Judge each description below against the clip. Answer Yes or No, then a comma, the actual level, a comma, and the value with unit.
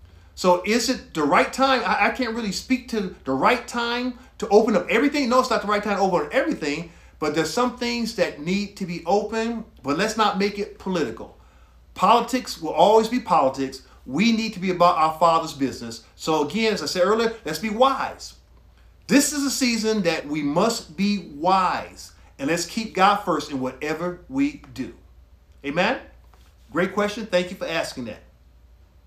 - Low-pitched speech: No, high, 205 Hz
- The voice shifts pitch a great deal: Yes, wide, 5.9 semitones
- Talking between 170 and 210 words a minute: Yes, average, 190 wpm